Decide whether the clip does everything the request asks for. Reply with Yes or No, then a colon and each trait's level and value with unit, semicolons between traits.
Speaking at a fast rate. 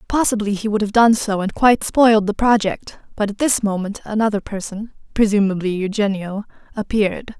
No: average, 160 wpm